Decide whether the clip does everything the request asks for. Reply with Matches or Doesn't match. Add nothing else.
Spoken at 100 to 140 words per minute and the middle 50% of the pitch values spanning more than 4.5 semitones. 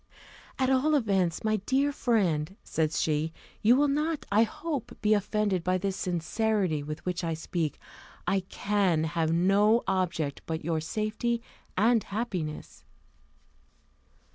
Matches